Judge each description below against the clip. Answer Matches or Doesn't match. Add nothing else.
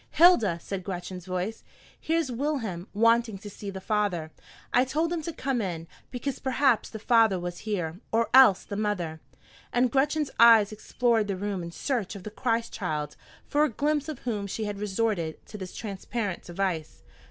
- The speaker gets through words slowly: Doesn't match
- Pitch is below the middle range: Doesn't match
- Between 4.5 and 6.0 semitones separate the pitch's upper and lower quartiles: Matches